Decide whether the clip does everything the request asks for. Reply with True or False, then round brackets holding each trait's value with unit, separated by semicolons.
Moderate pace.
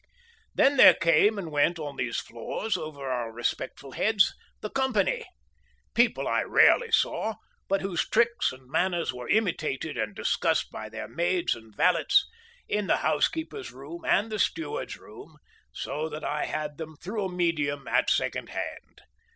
True (155 wpm)